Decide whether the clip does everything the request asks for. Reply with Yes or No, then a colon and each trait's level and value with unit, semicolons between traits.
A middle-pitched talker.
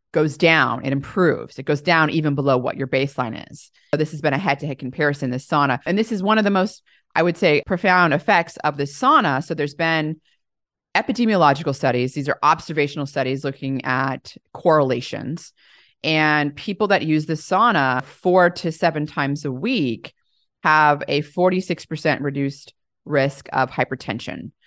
Yes: medium, 150 Hz